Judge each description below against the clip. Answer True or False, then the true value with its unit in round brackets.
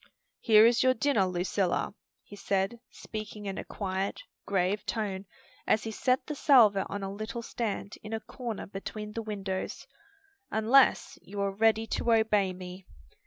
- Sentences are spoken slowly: False (160 wpm)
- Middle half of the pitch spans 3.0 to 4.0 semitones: False (2.5 semitones)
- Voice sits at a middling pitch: False (210 Hz)